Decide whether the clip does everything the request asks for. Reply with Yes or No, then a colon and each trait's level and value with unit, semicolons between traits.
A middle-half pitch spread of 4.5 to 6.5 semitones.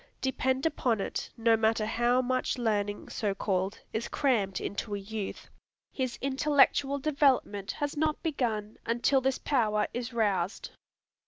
No: average, 4.1 semitones